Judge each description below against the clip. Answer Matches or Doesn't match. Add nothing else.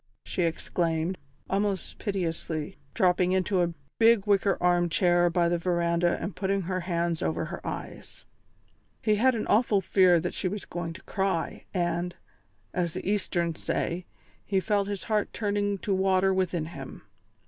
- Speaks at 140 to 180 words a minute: Matches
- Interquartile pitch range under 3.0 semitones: Matches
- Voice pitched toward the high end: Doesn't match